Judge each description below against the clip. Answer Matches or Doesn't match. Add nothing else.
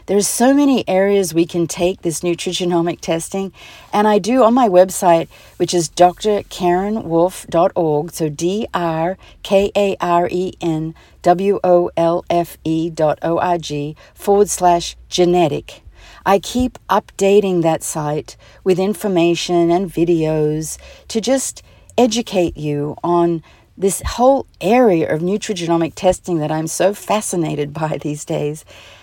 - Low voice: Doesn't match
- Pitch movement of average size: Matches